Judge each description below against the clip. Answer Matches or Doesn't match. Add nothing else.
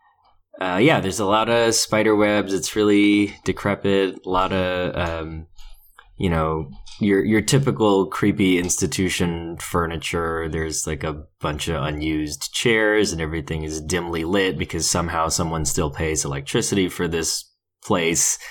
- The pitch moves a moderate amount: Matches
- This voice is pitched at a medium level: Doesn't match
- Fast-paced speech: Doesn't match